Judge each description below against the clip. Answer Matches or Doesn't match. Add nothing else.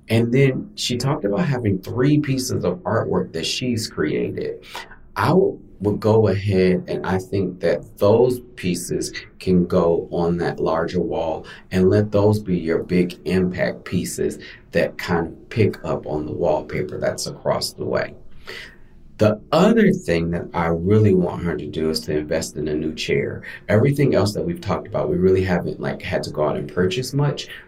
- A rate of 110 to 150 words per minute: Doesn't match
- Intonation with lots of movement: Matches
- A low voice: Matches